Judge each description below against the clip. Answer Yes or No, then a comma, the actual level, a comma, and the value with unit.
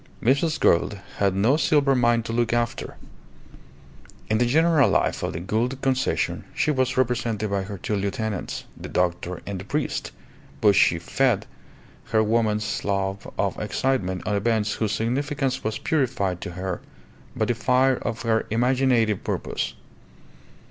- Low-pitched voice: Yes, low, 115 Hz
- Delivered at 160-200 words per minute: No, average, 150 wpm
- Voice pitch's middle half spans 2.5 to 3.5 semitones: No, average, 4.4 semitones